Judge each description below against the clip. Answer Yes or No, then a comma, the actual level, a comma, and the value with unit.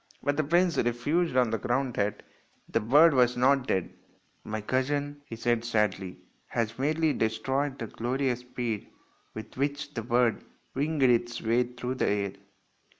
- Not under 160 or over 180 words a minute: Yes, average, 165 wpm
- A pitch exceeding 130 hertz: No, low, 125 Hz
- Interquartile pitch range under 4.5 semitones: Yes, average, 3.7 semitones